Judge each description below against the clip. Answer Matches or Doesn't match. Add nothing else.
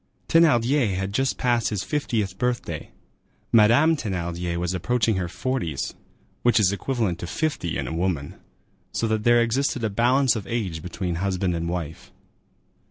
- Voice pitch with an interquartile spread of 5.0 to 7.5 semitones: Matches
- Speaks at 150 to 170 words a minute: Matches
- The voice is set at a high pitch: Doesn't match